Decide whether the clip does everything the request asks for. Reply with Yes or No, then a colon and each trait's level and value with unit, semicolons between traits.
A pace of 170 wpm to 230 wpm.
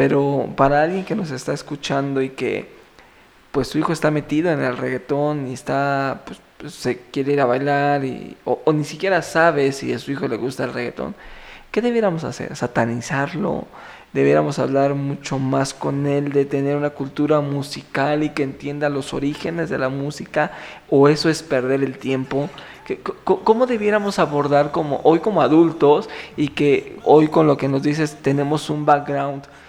Yes: average, 180 wpm